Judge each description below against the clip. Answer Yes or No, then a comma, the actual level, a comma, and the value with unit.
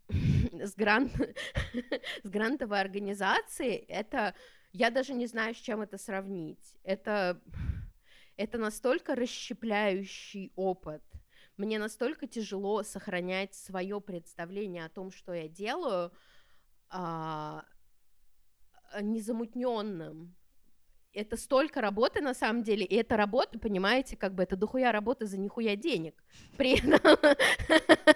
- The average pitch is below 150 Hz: No, high, 210 Hz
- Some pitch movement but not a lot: Yes, average, 4.2 semitones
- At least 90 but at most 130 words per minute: Yes, average, 115 wpm